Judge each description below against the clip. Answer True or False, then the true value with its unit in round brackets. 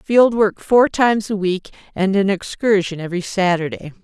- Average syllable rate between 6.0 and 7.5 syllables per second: False (5.0 syllables/s)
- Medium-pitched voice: False (195 Hz)